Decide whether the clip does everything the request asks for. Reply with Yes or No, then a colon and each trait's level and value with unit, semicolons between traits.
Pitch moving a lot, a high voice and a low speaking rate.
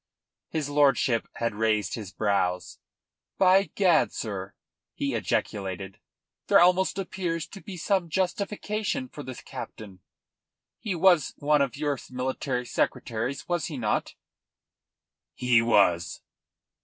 No: wide, 8.5 semitones; medium, 140 Hz; slow, 120 wpm